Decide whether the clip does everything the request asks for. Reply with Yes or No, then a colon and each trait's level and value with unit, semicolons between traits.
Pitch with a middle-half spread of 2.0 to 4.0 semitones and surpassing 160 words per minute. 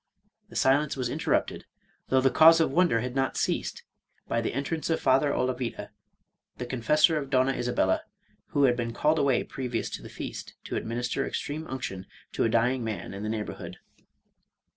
Yes: average, 3.1 semitones; average, 180 wpm